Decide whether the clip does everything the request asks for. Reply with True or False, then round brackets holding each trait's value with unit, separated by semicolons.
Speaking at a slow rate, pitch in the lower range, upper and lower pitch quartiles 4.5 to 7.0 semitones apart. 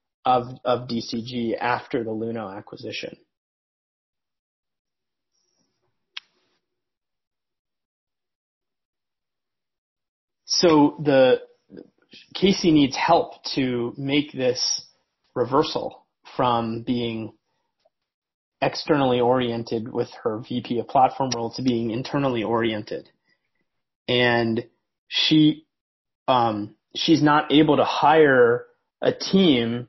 False (80 wpm; 125 Hz; 4.1 semitones)